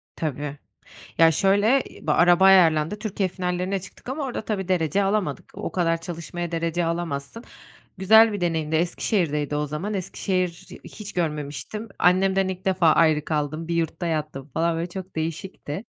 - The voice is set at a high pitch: No, medium, 175 Hz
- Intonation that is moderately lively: Yes, average, 3.4 semitones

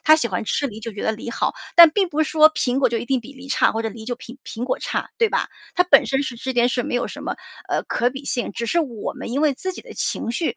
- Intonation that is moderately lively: Yes, average, 4.1 semitones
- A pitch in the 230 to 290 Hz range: Yes, very high, 255 Hz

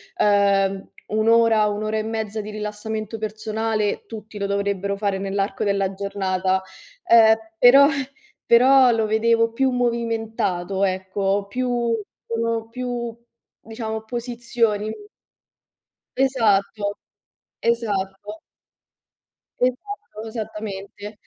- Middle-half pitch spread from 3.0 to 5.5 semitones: No, narrow, 2.4 semitones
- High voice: Yes, high, 215 Hz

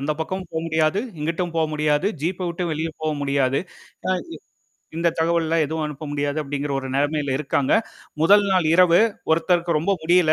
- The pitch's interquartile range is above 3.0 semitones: No, narrow, 2.6 semitones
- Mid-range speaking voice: Yes, medium, 160 Hz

